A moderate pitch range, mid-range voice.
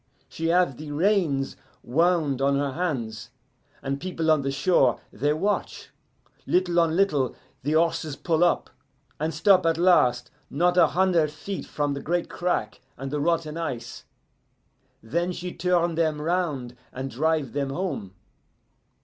Yes: average, 4.2 semitones; medium, 155 Hz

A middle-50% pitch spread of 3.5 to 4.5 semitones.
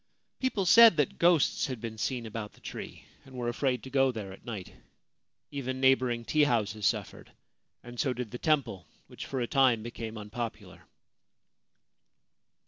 No: average, 3.1 semitones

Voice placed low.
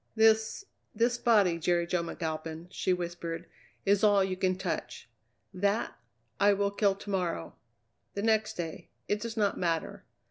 No: high, 190 Hz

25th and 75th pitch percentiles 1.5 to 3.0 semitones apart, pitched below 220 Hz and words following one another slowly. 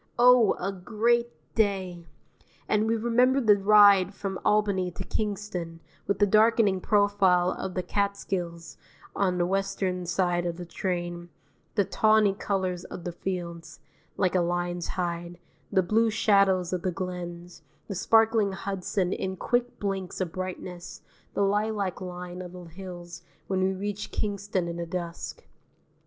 No: narrow, 2.6 semitones; high, 190 Hz; average, 145 wpm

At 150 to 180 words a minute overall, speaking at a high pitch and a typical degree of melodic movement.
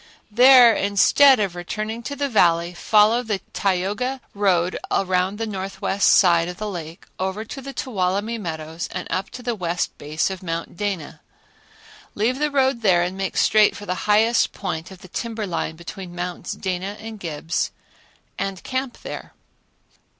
Yes: average, 165 wpm; high, 195 Hz; average, 4.0 semitones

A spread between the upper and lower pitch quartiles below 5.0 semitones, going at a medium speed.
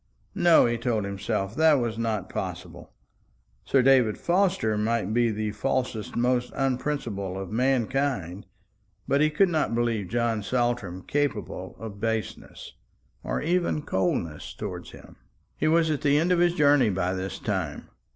No: wide, 5.4 semitones; average, 150 wpm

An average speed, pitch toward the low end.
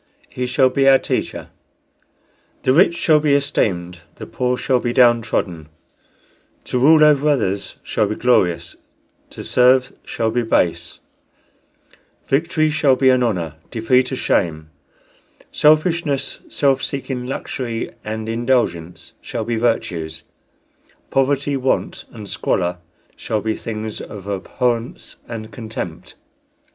No: slow, 125 wpm; low, 120 Hz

